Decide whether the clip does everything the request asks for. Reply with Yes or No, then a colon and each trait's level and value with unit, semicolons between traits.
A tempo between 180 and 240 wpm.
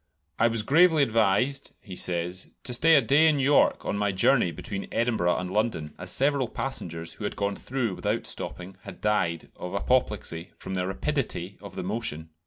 Yes: average, 185 wpm